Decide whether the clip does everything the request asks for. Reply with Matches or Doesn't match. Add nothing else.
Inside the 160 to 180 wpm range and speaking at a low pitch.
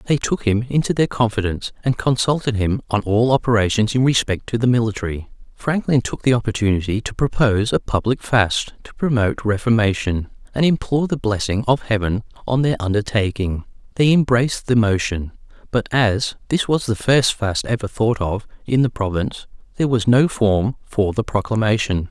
Matches